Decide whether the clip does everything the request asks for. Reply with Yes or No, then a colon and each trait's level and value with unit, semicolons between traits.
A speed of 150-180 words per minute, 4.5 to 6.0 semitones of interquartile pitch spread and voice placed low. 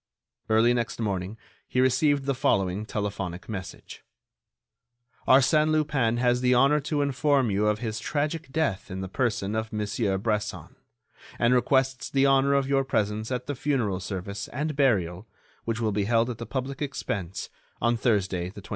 Yes: average, 165 wpm; average, 4.8 semitones; low, 120 Hz